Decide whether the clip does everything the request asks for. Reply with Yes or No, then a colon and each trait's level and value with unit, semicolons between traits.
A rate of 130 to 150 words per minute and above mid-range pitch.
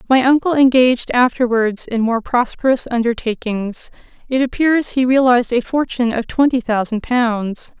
Yes: average, 140 wpm; high, 245 Hz